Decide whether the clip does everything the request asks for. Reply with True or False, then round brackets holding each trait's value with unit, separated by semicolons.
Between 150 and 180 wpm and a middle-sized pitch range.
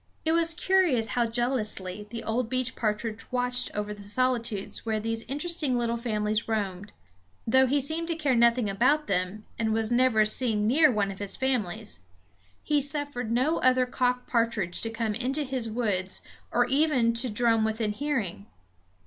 True (165 wpm; 3.3 semitones)